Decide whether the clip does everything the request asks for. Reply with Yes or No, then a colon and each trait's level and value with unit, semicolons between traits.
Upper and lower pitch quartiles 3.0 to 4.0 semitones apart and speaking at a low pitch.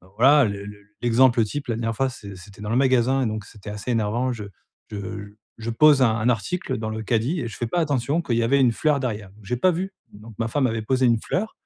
Yes: average, 3.4 semitones; low, 115 Hz